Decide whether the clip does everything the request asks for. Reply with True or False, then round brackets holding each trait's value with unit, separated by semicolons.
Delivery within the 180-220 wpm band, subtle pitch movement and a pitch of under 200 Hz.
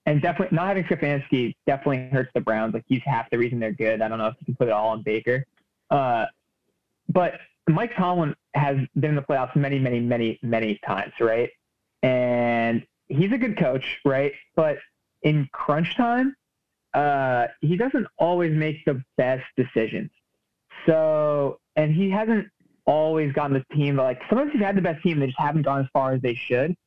False (190 wpm; 4.5 semitones; 140 Hz)